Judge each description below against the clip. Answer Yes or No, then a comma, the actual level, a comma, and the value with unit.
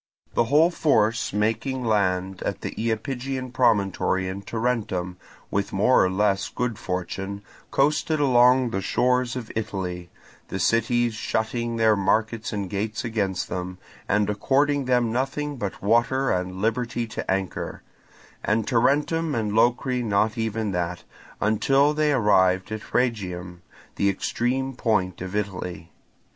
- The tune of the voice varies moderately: Yes, average, 4.3 semitones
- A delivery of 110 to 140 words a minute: Yes, slow, 135 wpm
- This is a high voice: No, low, 110 Hz